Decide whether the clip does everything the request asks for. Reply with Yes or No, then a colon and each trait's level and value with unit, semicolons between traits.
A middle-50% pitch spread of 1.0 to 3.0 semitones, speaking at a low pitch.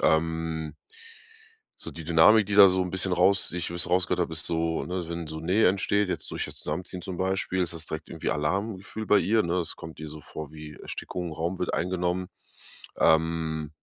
Yes: narrow, 2.5 semitones; very low, 85 Hz